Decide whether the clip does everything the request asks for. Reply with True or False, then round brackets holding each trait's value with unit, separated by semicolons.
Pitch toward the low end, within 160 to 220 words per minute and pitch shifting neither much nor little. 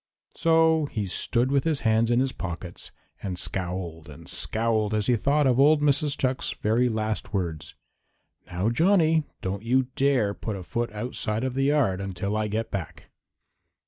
False (115 Hz; 170 wpm; 5.7 semitones)